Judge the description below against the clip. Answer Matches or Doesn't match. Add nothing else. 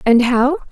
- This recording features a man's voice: Doesn't match